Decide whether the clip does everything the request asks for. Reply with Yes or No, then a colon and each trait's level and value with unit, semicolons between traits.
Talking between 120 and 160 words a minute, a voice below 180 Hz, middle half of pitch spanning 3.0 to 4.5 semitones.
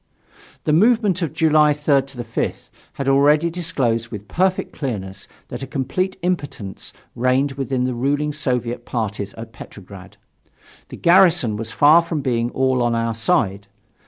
No: average, 145 wpm; low, 135 Hz; average, 4.9 semitones